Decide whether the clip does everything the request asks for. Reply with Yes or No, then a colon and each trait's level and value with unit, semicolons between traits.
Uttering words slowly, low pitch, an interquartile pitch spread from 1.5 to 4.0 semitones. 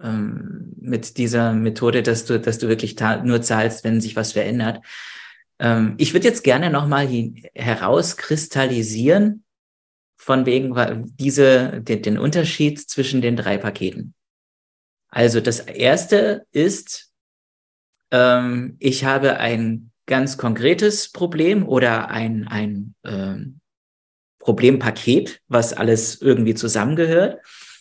Yes: slow, 115 wpm; low, 120 Hz; average, 3.4 semitones